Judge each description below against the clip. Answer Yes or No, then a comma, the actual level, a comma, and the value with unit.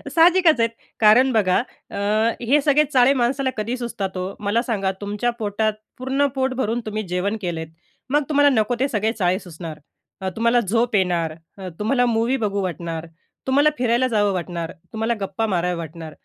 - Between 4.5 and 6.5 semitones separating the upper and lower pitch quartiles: Yes, average, 5.0 semitones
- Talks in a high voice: Yes, high, 220 Hz